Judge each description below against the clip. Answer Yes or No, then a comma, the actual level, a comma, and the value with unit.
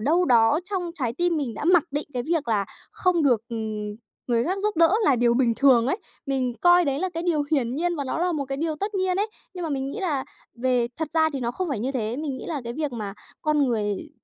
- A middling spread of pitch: No, wide, 5.9 semitones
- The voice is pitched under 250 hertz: No, very high, 280 Hz